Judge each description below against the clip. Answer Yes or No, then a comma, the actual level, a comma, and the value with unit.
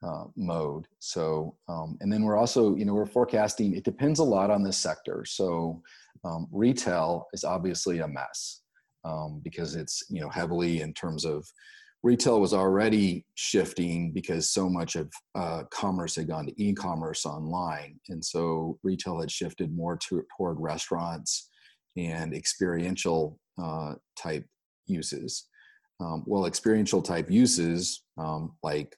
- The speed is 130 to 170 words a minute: Yes, average, 150 wpm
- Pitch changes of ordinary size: Yes, average, 4.1 semitones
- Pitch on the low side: Yes, very low, 85 Hz